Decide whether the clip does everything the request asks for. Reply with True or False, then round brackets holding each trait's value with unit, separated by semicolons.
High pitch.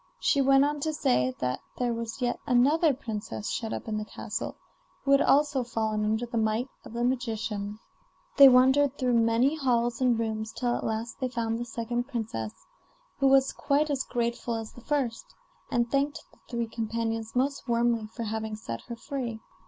True (235 Hz)